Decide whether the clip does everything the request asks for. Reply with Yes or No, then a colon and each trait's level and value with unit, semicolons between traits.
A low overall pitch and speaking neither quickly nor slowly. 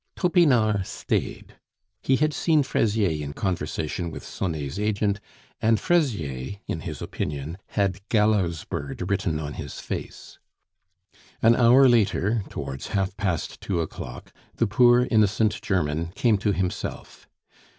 No: low, 100 Hz; slow, 130 wpm